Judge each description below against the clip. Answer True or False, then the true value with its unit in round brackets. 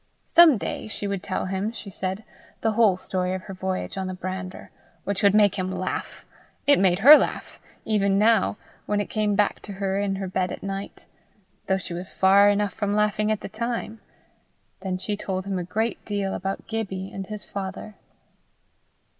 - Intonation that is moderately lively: False (2.0 semitones)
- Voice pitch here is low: False (195 Hz)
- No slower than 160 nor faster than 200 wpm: True (190 wpm)